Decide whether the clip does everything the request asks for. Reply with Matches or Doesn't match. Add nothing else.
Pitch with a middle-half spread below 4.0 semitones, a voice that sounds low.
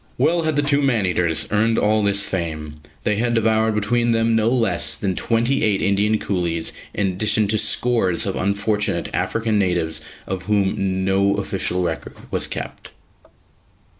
Matches